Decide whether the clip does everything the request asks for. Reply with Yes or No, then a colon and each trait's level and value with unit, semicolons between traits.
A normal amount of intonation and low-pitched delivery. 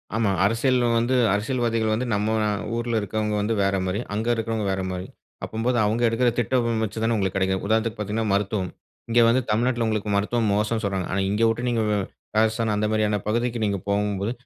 No: narrow, 2.1 semitones; low, 110 Hz